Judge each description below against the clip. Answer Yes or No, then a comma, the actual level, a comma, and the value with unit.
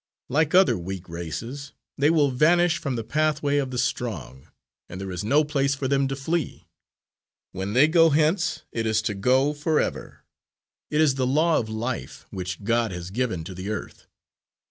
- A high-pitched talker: No, low, 130 Hz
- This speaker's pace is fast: No, average, 180 wpm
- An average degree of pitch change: No, wide, 6.5 semitones